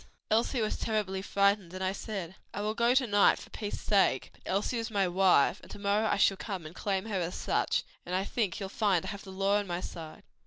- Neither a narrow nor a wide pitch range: No, narrow, 2.1 semitones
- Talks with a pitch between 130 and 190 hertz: No, high, 200 Hz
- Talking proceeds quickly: Yes, fast, 245 wpm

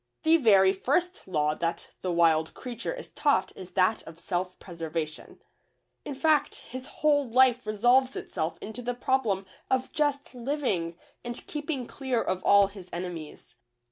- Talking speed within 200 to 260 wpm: No, average, 150 wpm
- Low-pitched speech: No, high, 225 Hz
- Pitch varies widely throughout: Yes, wide, 6.9 semitones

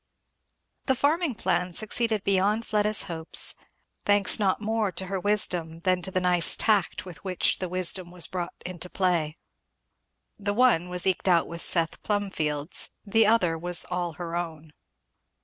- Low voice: No, medium, 185 Hz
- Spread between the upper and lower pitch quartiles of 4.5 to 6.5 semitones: No, average, 3.2 semitones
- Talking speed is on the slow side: No, average, 155 wpm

